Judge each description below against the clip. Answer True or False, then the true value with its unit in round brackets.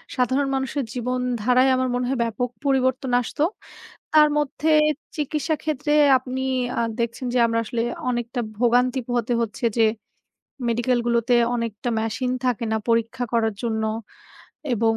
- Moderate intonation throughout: False (2.1 semitones)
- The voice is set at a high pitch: True (245 Hz)